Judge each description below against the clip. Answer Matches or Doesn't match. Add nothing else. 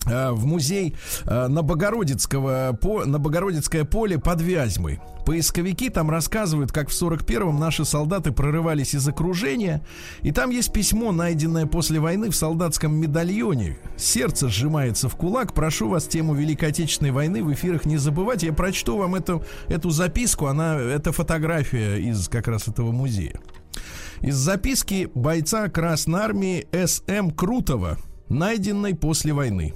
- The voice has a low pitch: Doesn't match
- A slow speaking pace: Doesn't match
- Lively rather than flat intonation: Doesn't match